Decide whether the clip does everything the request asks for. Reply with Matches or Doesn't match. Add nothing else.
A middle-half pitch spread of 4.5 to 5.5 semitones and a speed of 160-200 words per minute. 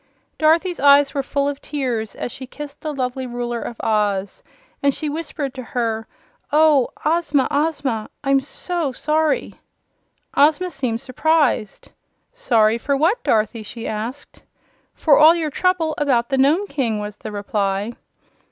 Doesn't match